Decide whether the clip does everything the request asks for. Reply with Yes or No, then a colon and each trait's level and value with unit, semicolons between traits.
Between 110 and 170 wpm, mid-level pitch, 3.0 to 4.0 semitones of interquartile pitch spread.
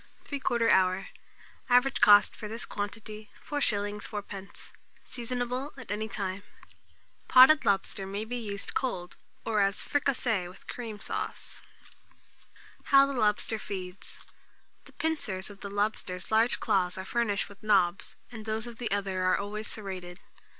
No: average, 145 wpm; high, 210 Hz; average, 3.3 semitones